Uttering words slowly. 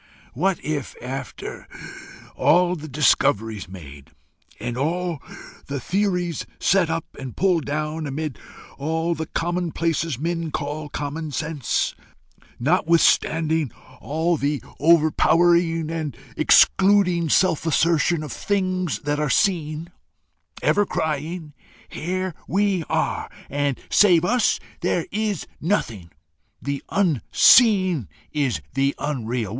Yes: slow, 110 wpm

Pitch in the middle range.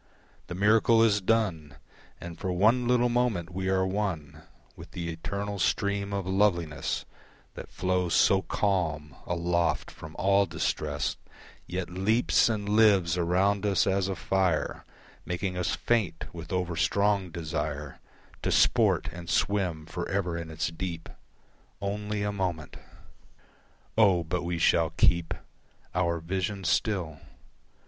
No: very low, 90 Hz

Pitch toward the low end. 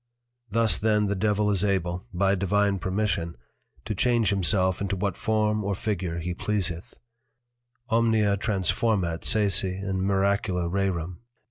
Yes: low, 100 Hz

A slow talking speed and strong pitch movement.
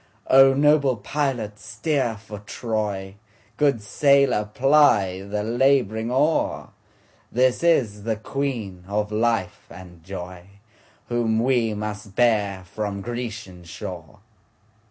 No: slow, 95 wpm; average, 4.0 semitones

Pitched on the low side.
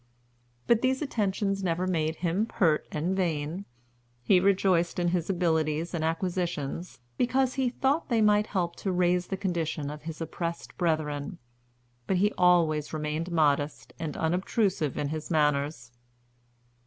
No: medium, 170 Hz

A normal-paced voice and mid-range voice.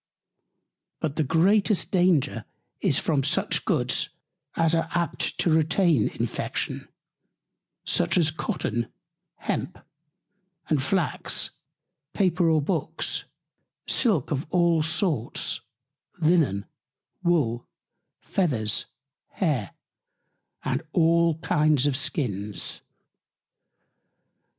No: slow, 90 wpm; medium, 160 Hz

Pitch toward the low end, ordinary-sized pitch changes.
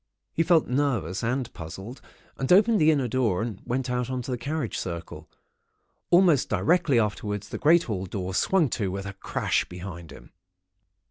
No: low, 120 Hz; wide, 7.1 semitones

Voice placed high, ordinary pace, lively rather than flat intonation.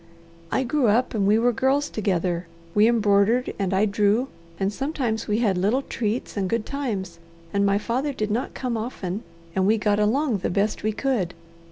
No: high, 215 Hz; average, 190 wpm; average, 3.7 semitones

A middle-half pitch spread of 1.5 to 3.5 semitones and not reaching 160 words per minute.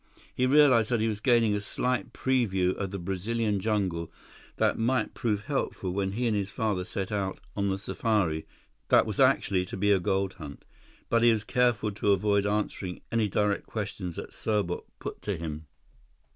No: average, 2.9 semitones; average, 185 wpm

